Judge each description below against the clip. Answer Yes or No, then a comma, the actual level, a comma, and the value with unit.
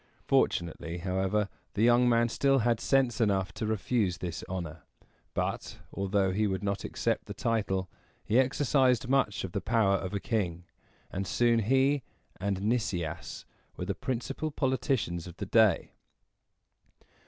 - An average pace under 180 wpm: Yes, average, 145 wpm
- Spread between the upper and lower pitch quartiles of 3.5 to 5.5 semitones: Yes, average, 4.4 semitones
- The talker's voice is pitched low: Yes, low, 105 Hz